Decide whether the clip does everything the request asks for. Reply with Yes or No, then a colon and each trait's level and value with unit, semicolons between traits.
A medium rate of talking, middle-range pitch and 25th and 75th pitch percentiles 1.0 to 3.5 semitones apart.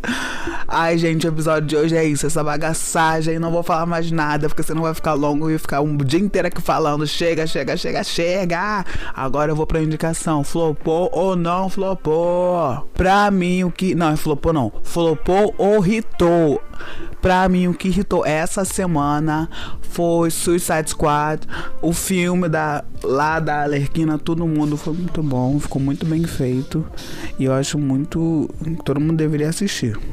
Yes: average, 165 wpm; medium, 160 Hz; narrow, 2.6 semitones